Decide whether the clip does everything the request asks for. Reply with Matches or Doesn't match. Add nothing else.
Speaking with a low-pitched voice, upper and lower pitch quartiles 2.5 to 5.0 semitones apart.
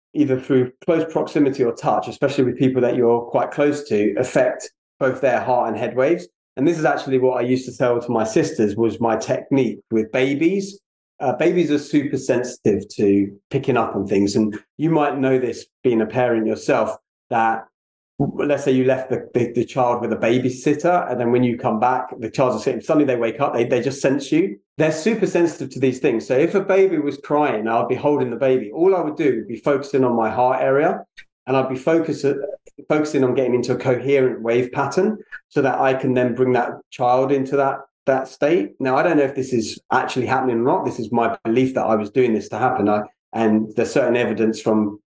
Matches